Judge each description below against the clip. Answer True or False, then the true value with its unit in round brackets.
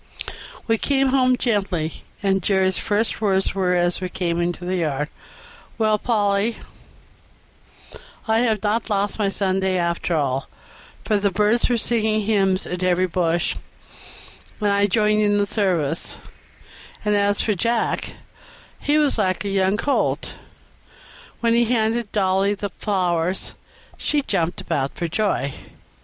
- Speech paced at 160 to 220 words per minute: False (140 wpm)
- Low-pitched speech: False (200 Hz)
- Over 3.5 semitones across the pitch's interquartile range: False (3.2 semitones)